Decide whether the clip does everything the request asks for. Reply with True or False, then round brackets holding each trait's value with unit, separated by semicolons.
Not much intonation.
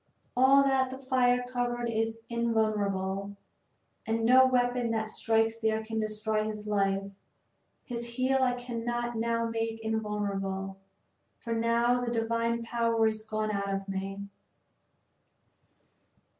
True (2.0 semitones)